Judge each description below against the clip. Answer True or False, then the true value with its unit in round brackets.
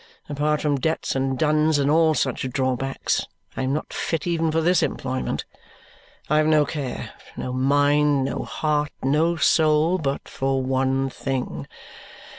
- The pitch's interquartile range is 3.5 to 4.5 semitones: False (2.6 semitones)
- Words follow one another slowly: False (150 wpm)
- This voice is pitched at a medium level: True (145 Hz)